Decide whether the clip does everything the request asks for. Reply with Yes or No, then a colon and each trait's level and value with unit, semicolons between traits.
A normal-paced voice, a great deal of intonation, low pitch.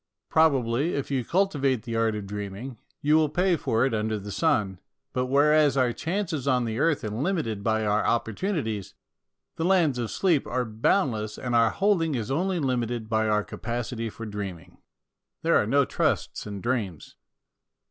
Yes: average, 170 wpm; wide, 5.7 semitones; low, 120 Hz